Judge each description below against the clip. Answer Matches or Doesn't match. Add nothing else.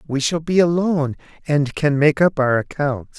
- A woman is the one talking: Doesn't match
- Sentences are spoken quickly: Doesn't match